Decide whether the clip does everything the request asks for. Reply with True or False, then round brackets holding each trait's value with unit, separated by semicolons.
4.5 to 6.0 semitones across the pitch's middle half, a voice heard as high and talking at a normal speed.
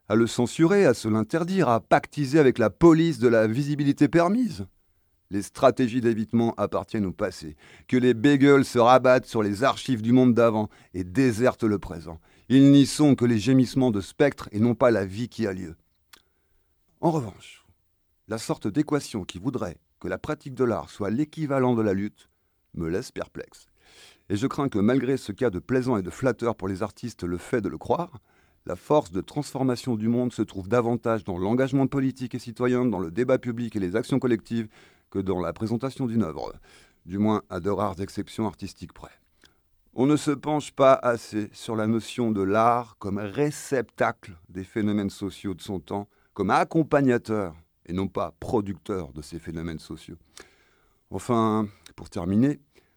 False (5.0 semitones; 115 Hz; 180 wpm)